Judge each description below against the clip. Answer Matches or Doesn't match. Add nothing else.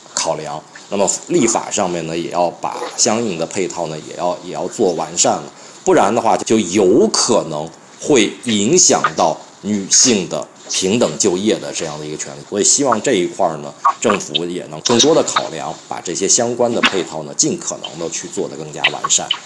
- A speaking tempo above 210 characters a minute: Matches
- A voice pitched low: Matches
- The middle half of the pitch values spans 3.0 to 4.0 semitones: Doesn't match